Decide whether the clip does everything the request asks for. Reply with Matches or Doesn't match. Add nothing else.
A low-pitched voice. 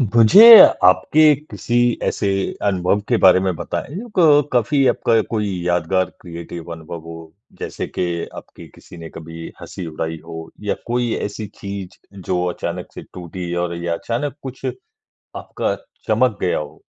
Matches